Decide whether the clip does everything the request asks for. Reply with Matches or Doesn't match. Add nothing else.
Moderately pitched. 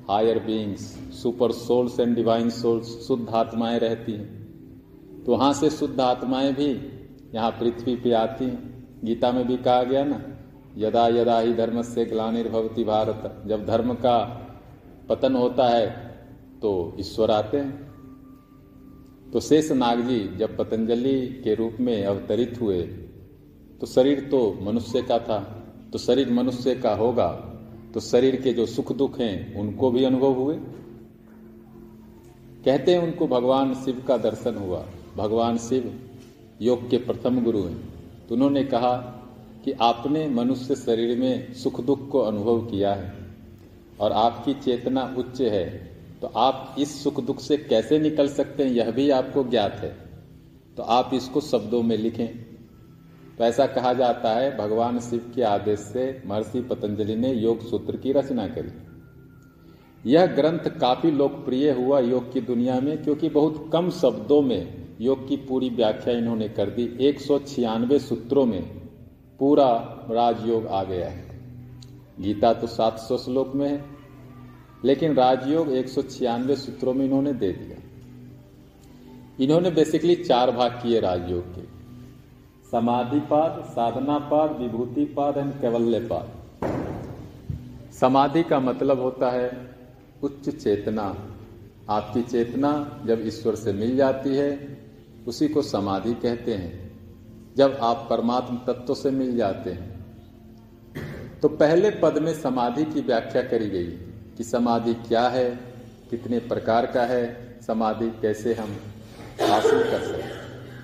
Doesn't match